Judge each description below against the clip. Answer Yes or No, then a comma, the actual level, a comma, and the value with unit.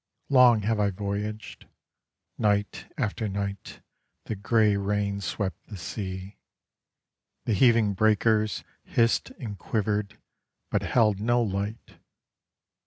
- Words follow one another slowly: Yes, slow, 105 wpm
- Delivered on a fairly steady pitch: Yes, narrow, 1.7 semitones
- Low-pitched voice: Yes, low, 105 Hz